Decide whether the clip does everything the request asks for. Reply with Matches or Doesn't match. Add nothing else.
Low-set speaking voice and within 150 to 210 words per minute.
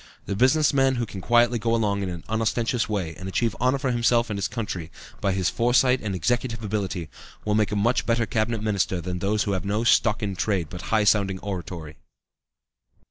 Matches